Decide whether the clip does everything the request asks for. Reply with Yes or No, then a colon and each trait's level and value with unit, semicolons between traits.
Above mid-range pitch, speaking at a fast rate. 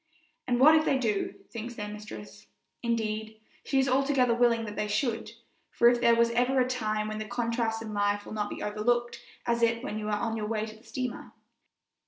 Yes: high, 230 Hz; fast, 215 wpm